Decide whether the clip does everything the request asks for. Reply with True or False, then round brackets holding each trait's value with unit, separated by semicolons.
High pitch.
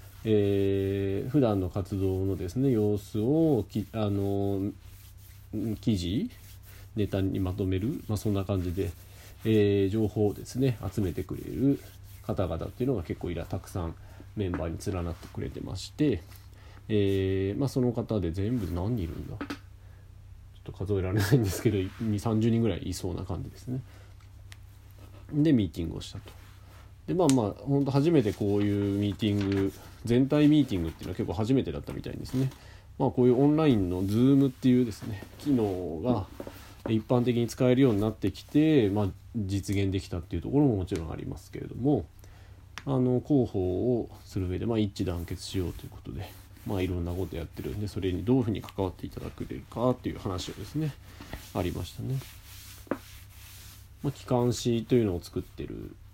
False (100 Hz)